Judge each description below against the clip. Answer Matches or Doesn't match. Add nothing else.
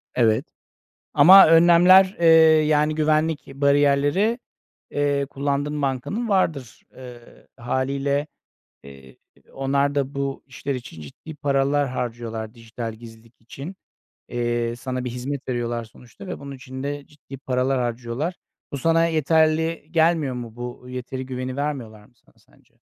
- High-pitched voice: Doesn't match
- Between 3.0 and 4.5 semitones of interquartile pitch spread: Matches